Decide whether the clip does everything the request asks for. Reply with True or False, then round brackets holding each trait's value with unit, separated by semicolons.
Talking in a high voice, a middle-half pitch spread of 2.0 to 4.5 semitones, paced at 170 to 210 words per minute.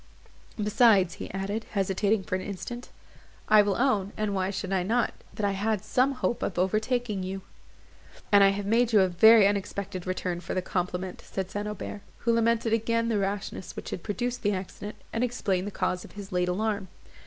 True (205 Hz; 2.8 semitones; 195 wpm)